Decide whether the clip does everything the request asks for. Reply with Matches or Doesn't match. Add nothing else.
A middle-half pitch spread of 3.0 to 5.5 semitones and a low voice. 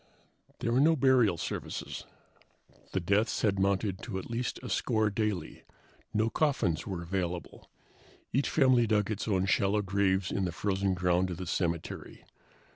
Matches